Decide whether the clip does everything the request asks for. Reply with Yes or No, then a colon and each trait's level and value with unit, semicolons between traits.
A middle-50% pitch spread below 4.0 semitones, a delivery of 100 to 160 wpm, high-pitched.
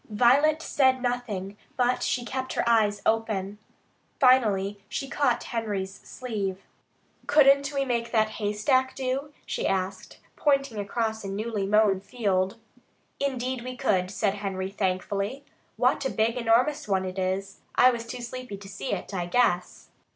No: average, 4.4 semitones; average, 150 wpm; high, 225 Hz